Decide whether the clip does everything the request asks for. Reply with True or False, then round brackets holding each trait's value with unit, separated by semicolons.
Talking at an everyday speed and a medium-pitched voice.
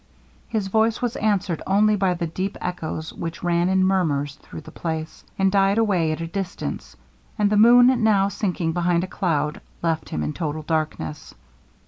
True (175 wpm; 180 Hz)